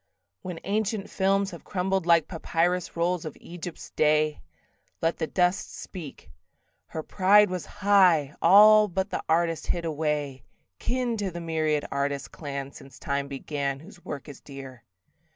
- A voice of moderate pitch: Yes, medium, 165 Hz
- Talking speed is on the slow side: No, average, 150 wpm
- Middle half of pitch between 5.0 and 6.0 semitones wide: No, average, 4.4 semitones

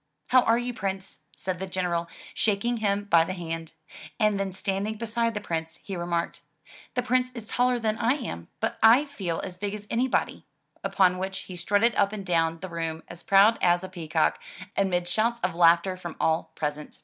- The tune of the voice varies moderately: Yes, average, 4.2 semitones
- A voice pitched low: No, high, 190 Hz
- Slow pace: No, average, 195 wpm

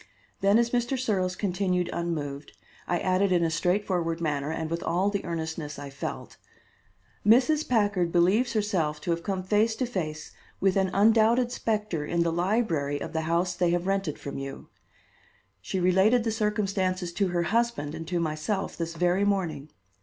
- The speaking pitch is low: No, medium, 180 Hz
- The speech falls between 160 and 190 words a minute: Yes, average, 170 wpm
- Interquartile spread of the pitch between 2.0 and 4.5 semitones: Yes, average, 3.9 semitones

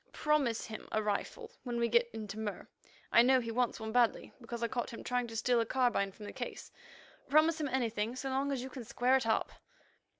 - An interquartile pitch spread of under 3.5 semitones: Yes, average, 2.7 semitones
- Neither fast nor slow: No, fast, 225 wpm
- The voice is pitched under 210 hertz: No, high, 240 Hz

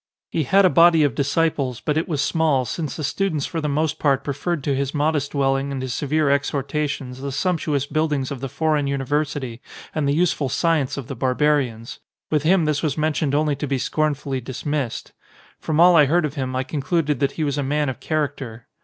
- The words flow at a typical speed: No, fast, 210 wpm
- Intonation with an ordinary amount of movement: No, narrow, 2.3 semitones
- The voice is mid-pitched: Yes, medium, 145 Hz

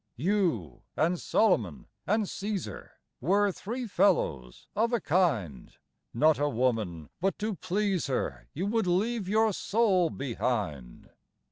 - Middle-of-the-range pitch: Yes, medium, 180 Hz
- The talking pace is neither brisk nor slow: No, slow, 125 wpm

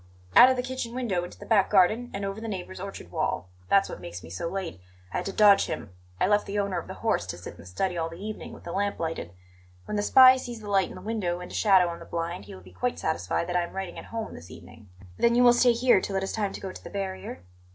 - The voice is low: No, high, 195 Hz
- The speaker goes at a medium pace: No, fast, 295 wpm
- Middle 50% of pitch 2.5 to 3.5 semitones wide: No, average, 4.3 semitones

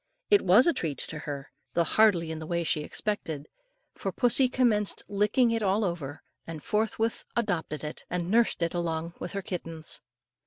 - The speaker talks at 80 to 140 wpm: No, average, 180 wpm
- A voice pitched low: No, medium, 175 Hz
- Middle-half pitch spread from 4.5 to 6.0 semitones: Yes, average, 5.2 semitones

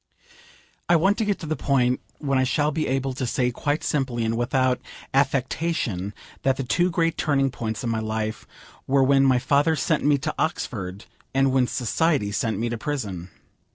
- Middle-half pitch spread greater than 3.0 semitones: Yes, average, 3.8 semitones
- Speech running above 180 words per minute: Yes, average, 190 wpm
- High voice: No, low, 135 Hz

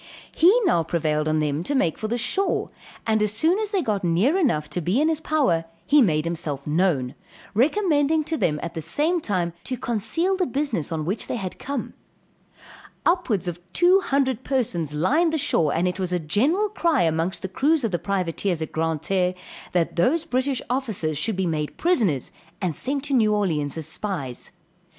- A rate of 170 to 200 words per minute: Yes, average, 190 wpm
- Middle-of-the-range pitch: No, high, 205 Hz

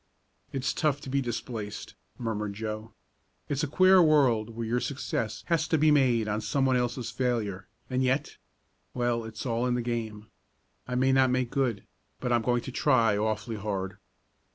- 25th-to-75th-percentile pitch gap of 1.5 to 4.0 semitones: Yes, average, 3.2 semitones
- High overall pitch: No, low, 120 Hz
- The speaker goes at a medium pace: Yes, average, 175 wpm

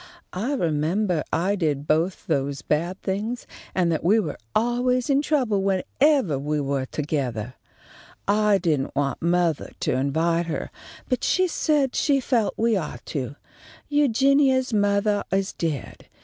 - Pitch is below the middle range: No, high, 190 Hz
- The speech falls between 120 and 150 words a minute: Yes, average, 145 wpm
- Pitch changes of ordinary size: No, wide, 8.0 semitones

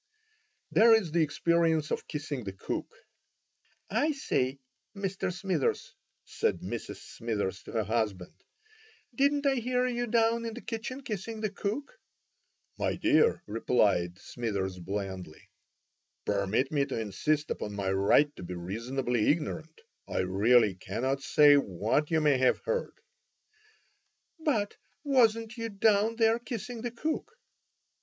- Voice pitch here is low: No, medium, 155 Hz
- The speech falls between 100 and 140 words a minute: Yes, slow, 135 wpm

